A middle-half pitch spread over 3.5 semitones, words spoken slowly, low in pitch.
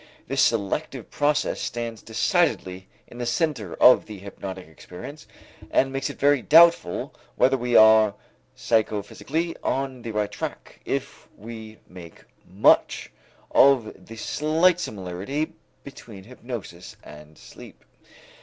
Yes: wide, 5.5 semitones; slow, 120 wpm; low, 115 Hz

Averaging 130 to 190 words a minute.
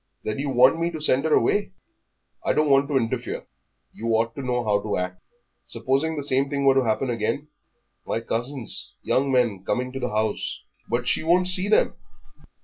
No: average, 200 wpm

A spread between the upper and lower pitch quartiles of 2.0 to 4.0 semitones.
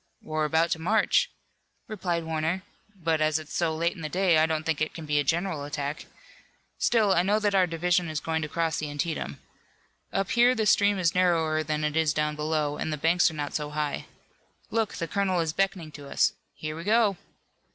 Yes: average, 3.1 semitones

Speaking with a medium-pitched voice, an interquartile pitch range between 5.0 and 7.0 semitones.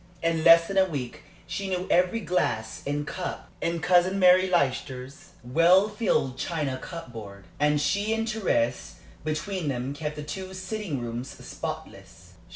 Yes: medium, 165 Hz; wide, 5.5 semitones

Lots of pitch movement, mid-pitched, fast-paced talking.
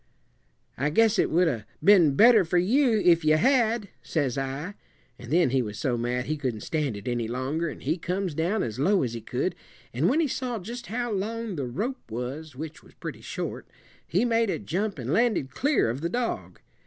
Yes: wide, 8.8 semitones; medium, 165 Hz; fast, 210 wpm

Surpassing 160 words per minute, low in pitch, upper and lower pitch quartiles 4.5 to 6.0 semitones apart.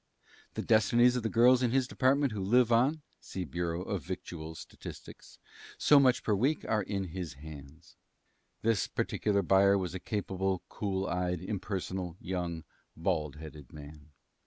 No: average, 155 wpm; very low, 95 Hz; average, 5.1 semitones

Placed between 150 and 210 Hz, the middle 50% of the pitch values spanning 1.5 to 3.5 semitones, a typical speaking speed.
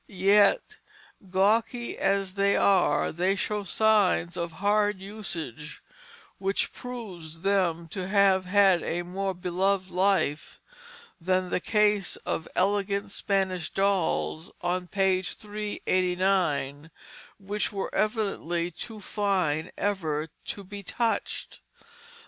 No: high, 190 Hz; narrow, 2.4 semitones; slow, 110 wpm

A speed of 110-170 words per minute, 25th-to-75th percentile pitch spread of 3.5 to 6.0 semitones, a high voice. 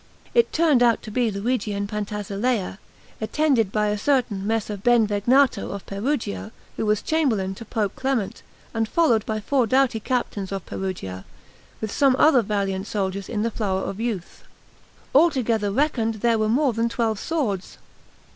Yes: average, 155 wpm; average, 3.8 semitones; high, 220 Hz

